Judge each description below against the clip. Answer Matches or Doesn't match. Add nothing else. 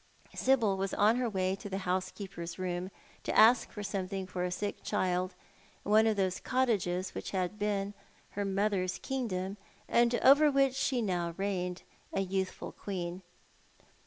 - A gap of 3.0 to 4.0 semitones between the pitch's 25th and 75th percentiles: Doesn't match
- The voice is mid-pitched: Doesn't match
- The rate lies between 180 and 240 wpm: Doesn't match